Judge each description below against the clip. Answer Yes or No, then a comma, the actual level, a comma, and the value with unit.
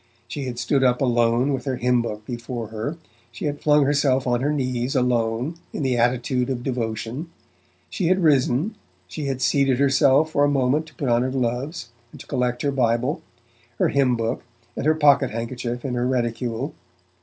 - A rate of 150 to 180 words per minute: No, average, 190 wpm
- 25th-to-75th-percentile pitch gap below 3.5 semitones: Yes, average, 2.8 semitones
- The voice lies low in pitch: Yes, low, 130 Hz